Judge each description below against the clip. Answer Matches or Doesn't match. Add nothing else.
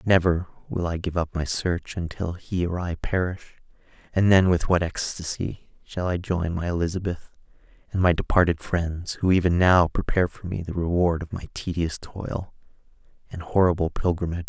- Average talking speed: Matches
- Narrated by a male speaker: Matches